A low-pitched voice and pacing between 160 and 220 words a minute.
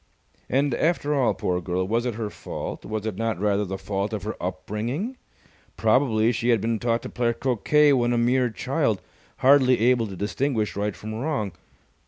Yes: low, 115 Hz; average, 185 wpm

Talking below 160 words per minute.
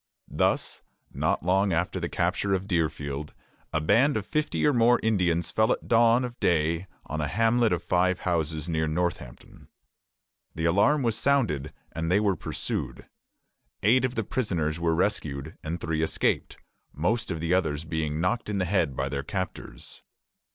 No: average, 165 wpm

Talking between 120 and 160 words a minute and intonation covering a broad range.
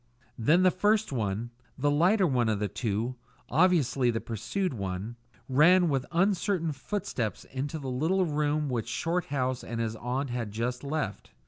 Yes: average, 150 wpm; wide, 6.2 semitones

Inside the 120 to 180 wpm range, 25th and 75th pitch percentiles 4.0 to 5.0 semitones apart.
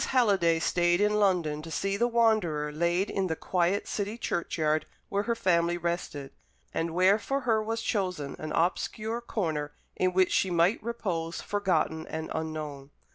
Yes: average, 160 wpm; average, 4.5 semitones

